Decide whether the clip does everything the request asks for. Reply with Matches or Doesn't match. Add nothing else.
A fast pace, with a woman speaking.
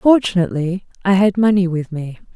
Doesn't match